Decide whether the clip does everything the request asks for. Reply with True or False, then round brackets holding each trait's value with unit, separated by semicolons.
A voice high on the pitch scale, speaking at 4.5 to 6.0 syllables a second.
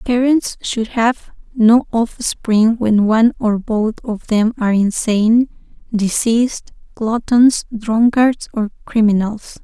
False (225 Hz; 3.7 syllables/s)